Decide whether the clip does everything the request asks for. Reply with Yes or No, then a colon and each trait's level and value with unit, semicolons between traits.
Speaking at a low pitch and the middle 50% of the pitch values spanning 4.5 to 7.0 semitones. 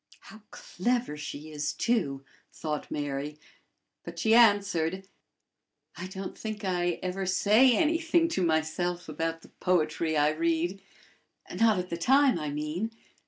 No: medium, 180 Hz; wide, 5.6 semitones